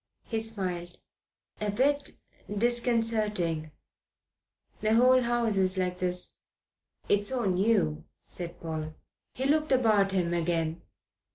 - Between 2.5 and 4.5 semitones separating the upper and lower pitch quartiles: No, average, 5.0 semitones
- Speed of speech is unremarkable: No, slow, 110 wpm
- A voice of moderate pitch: No, high, 205 Hz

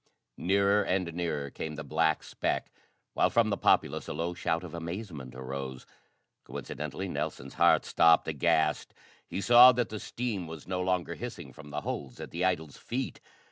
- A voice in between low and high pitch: No, very low, 85 Hz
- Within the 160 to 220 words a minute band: Yes, average, 170 wpm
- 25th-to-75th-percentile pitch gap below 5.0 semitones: Yes, average, 4.3 semitones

